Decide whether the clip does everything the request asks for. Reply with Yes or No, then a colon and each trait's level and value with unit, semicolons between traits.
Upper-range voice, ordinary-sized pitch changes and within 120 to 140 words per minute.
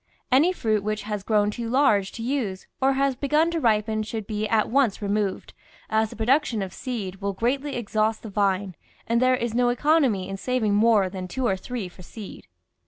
No: high, 220 Hz; average, 3.9 semitones; average, 200 wpm